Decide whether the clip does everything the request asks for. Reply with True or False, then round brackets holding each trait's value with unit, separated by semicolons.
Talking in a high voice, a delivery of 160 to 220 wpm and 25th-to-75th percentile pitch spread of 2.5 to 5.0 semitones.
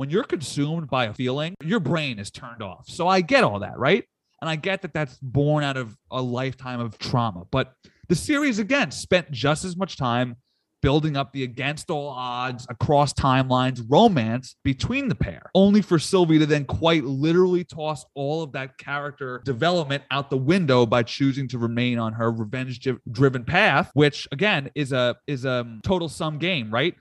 False (140 Hz; 190 wpm; 4.5 semitones)